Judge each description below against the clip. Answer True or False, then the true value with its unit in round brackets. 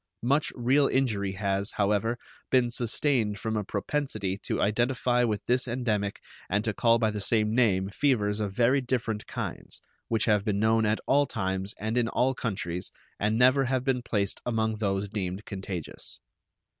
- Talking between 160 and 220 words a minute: True (170 wpm)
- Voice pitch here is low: True (110 Hz)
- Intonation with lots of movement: False (3.4 semitones)